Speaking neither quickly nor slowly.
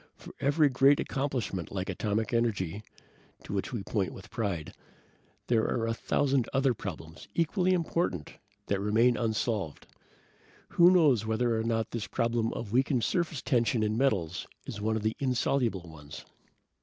Yes: average, 155 wpm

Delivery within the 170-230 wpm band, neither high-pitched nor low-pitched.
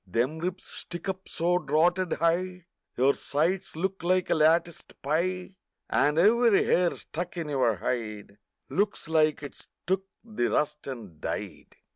No: average, 145 wpm; medium, 170 Hz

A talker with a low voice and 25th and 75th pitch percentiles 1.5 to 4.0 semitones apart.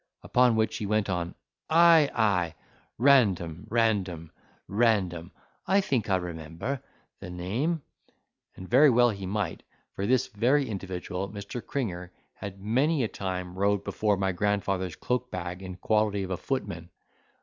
No: low, 100 Hz; average, 4.8 semitones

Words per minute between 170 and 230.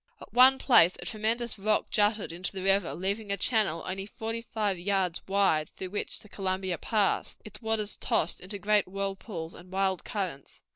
Yes: average, 180 wpm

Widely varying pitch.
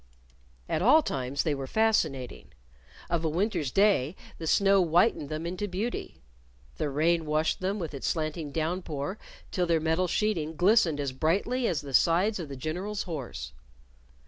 No: average, 4.3 semitones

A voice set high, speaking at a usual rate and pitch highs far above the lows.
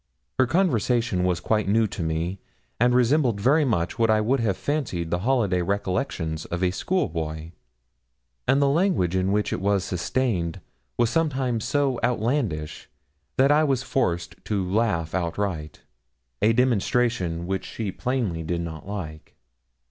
No: low, 105 Hz; average, 150 wpm; wide, 6.3 semitones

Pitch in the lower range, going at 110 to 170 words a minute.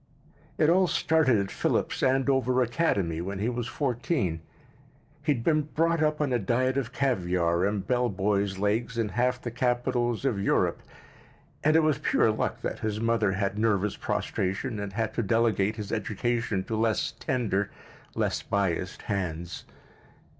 Yes: low, 115 Hz; average, 160 wpm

